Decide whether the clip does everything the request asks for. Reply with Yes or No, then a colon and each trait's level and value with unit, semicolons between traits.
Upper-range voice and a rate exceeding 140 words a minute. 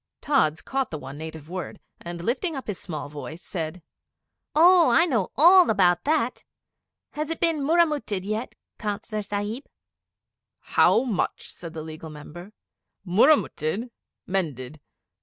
No: high, 205 Hz; slow, 135 wpm